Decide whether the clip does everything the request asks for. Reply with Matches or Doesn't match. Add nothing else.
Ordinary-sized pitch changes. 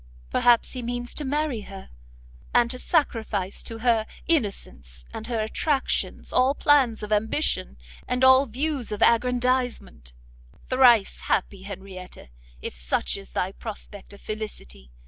Matches